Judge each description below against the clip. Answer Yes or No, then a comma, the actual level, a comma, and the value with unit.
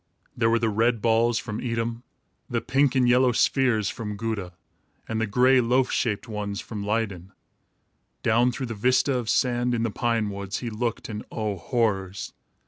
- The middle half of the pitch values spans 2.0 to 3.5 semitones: Yes, narrow, 2.5 semitones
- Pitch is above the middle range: No, low, 115 Hz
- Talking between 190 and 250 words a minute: No, average, 175 wpm